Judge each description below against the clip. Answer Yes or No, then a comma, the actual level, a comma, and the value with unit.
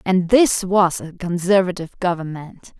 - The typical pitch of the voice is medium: Yes, medium, 180 Hz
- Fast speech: No, slow, 130 wpm